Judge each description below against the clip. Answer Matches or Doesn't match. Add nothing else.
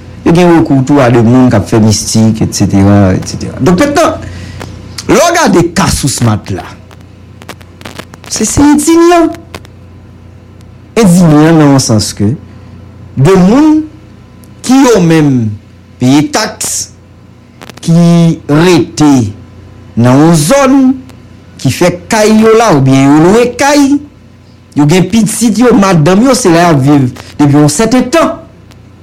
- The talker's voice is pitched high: Doesn't match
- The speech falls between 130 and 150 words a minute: Matches